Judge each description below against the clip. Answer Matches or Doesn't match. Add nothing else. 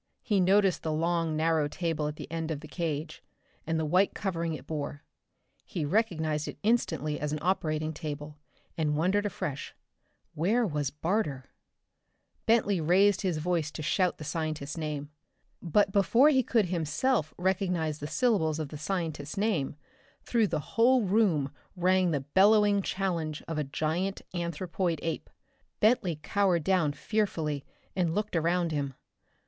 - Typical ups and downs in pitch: Matches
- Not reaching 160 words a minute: Matches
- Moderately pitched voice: Matches